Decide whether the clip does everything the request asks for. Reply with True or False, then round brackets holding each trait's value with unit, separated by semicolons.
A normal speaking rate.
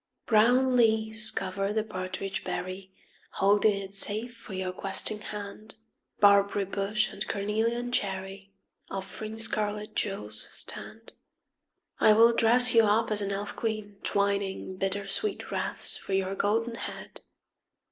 False (130 wpm)